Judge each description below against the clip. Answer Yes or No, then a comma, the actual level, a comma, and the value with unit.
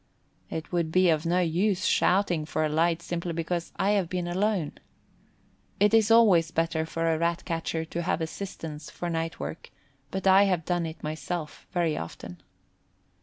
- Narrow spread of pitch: Yes, narrow, 2.2 semitones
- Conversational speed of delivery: Yes, average, 170 wpm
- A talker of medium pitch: Yes, medium, 170 Hz